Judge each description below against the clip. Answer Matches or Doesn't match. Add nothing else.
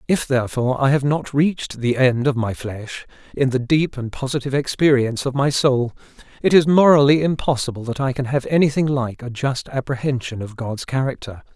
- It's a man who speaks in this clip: Matches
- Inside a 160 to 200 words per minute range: Matches